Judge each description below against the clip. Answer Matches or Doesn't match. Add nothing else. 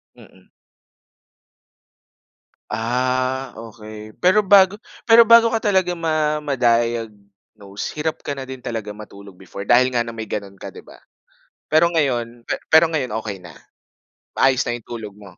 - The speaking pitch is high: Doesn't match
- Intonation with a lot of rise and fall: Matches